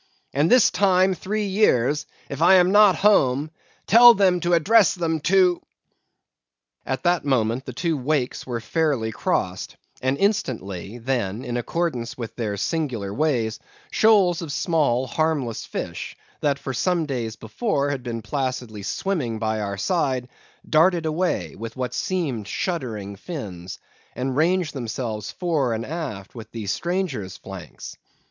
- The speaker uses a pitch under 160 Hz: Yes, medium, 140 Hz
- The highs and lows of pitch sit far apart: Yes, wide, 7.1 semitones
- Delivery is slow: No, average, 150 wpm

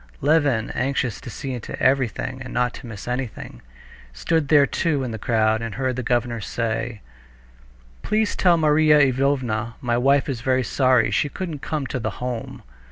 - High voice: No, low, 130 Hz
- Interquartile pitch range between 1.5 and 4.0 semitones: Yes, average, 3.2 semitones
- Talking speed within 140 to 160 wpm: No, average, 170 wpm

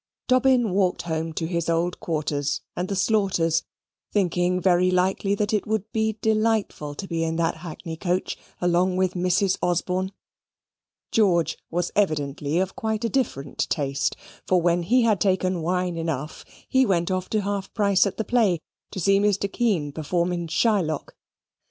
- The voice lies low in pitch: No, medium, 180 Hz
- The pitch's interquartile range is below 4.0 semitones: Yes, average, 3.4 semitones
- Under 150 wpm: No, average, 165 wpm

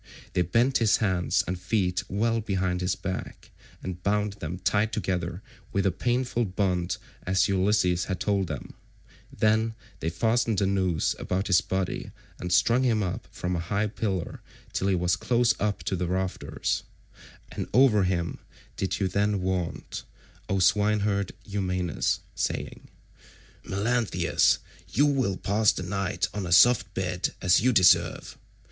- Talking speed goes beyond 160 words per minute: No, average, 150 wpm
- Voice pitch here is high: No, very low, 95 Hz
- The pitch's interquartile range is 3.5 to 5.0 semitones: No, average, 2.8 semitones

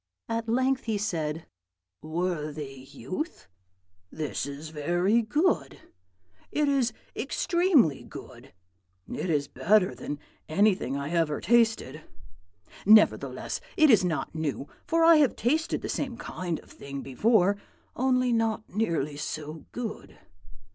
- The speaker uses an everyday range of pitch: No, wide, 7.6 semitones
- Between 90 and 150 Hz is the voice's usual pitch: No, high, 195 Hz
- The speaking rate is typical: No, slow, 120 wpm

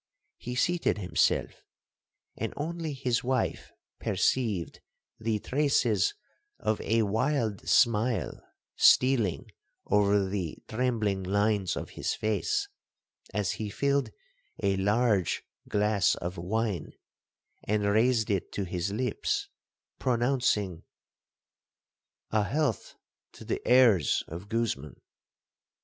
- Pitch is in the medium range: No, low, 110 Hz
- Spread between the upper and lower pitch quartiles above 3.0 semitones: Yes, average, 4.0 semitones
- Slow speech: Yes, slow, 100 wpm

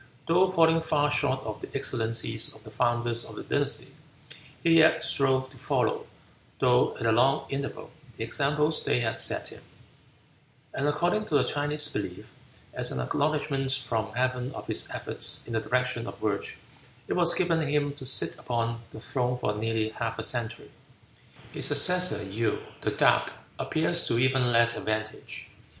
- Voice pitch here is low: Yes, low, 130 Hz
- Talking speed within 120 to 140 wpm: No, average, 165 wpm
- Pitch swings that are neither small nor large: Yes, average, 4.4 semitones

